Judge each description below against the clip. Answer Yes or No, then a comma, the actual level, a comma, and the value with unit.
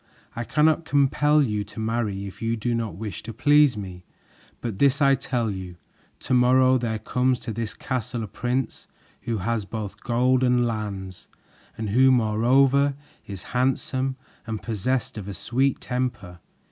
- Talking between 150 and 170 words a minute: Yes, average, 160 wpm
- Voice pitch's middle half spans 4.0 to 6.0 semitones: No, average, 3.4 semitones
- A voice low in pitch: Yes, low, 120 Hz